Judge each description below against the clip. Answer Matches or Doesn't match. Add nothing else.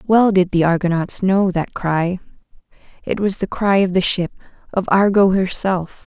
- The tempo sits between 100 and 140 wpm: Doesn't match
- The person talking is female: Matches